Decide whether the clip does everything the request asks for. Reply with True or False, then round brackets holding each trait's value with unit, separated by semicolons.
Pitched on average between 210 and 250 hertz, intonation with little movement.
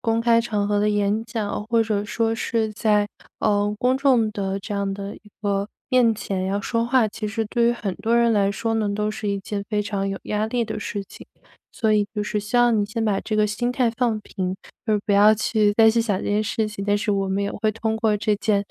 True (215 Hz; 1.9 semitones)